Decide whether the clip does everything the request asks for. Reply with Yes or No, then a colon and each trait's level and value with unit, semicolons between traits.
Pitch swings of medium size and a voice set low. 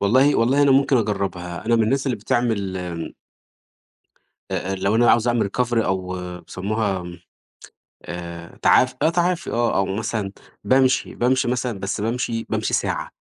Yes: average, 4.4 semitones; low, 115 Hz